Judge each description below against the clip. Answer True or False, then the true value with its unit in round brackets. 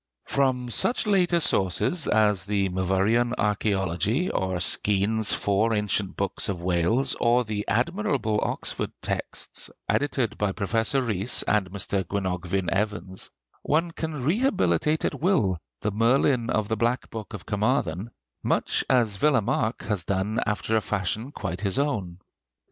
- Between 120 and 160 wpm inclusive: True (135 wpm)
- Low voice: True (105 Hz)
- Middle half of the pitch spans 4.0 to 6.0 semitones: True (4.6 semitones)